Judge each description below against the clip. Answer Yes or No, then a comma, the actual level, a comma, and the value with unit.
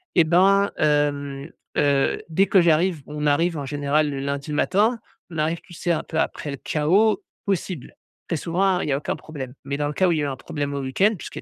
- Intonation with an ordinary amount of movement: Yes, average, 3.8 semitones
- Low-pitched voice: No, medium, 155 Hz